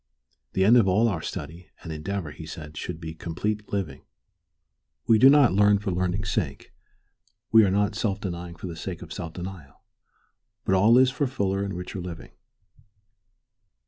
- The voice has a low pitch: Yes, very low, 95 Hz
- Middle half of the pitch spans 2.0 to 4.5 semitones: Yes, average, 3.4 semitones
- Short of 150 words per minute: No, average, 175 wpm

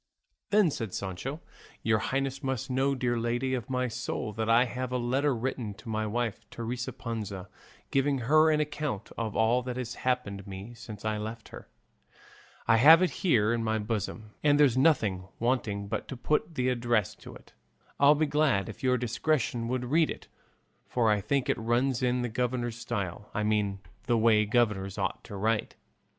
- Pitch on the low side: Yes, low, 120 Hz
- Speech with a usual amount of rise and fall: Yes, average, 3.3 semitones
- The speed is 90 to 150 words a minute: No, average, 185 wpm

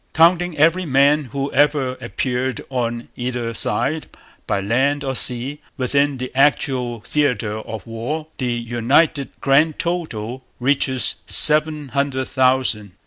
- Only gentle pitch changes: No, average, 3.3 semitones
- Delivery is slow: Yes, slow, 125 wpm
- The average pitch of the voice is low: Yes, low, 130 Hz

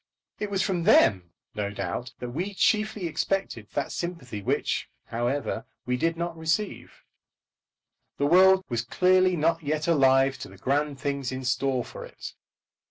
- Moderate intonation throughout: No, wide, 5.9 semitones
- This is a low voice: No, medium, 145 Hz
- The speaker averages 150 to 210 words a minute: Yes, average, 155 wpm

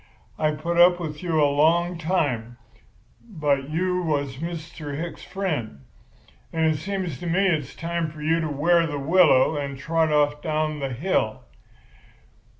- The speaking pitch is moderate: Yes, medium, 155 Hz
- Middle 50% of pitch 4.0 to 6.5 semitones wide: No, average, 2.9 semitones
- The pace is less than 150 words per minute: No, average, 155 wpm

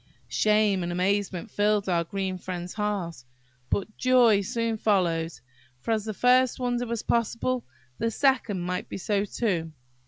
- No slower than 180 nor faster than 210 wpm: No, average, 150 wpm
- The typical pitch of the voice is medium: No, high, 205 Hz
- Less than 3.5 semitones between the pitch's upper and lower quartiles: No, average, 4.1 semitones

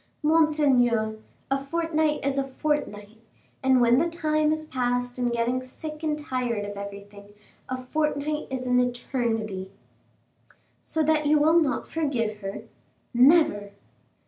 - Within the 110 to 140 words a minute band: Yes, slow, 135 wpm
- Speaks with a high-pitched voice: Yes, very high, 260 Hz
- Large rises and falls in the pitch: No, average, 4.7 semitones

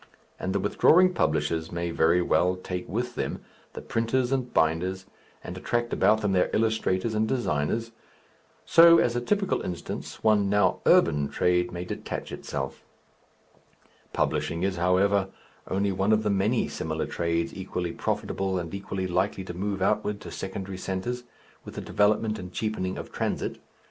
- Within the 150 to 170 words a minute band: Yes, average, 155 wpm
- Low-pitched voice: Yes, very low, 95 Hz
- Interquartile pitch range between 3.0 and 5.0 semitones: Yes, average, 3.7 semitones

